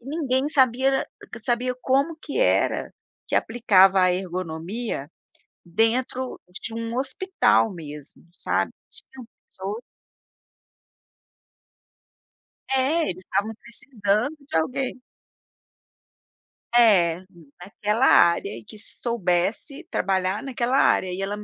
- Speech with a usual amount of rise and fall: No, wide, 5.8 semitones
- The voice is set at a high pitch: Yes, high, 225 Hz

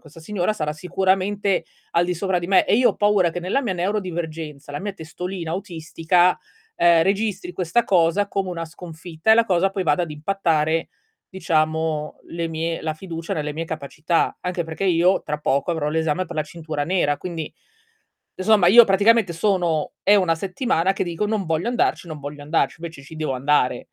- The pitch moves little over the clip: No, average, 3.2 semitones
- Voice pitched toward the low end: No, medium, 170 Hz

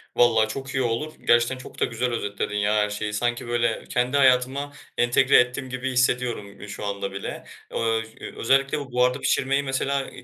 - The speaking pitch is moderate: No, low, 125 Hz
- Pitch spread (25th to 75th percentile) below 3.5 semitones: Yes, average, 2.9 semitones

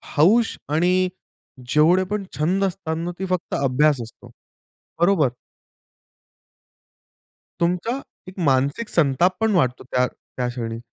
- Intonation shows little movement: No, wide, 5.5 semitones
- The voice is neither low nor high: Yes, medium, 170 Hz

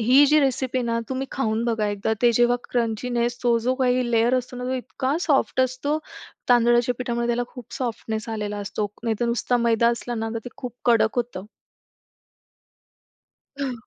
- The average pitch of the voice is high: Yes, high, 240 Hz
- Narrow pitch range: Yes, narrow, 1.7 semitones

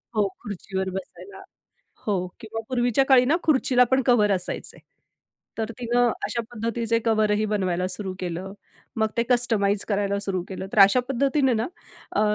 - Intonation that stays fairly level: No, average, 3.7 semitones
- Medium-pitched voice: No, high, 220 Hz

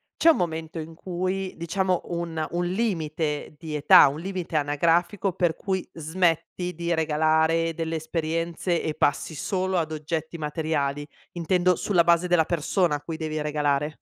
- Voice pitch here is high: No, medium, 165 Hz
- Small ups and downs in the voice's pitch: Yes, narrow, 2.2 semitones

